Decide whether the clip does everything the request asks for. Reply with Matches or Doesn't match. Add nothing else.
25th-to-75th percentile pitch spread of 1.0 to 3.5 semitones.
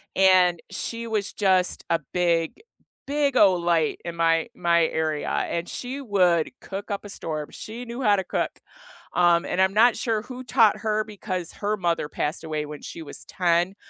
Doesn't match